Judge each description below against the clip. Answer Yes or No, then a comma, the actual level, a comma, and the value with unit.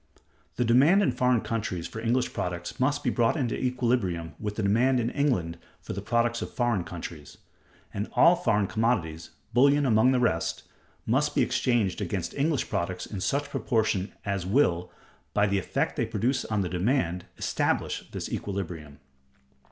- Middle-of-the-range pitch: No, low, 110 Hz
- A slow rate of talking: No, average, 165 wpm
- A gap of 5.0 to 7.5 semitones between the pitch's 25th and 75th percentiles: Yes, wide, 5.5 semitones